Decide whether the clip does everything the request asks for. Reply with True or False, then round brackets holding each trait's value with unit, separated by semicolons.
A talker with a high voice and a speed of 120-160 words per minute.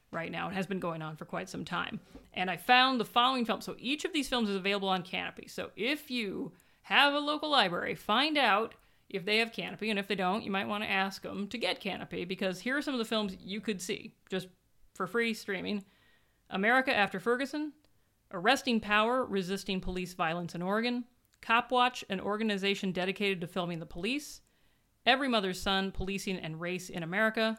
False (205 Hz; 200 wpm)